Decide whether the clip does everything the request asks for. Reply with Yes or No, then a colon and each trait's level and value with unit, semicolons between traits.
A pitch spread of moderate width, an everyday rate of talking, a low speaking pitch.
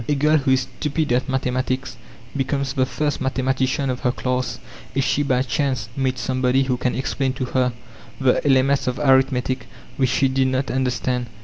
No: narrow, 1.1 semitones; average, 180 wpm; low, 130 Hz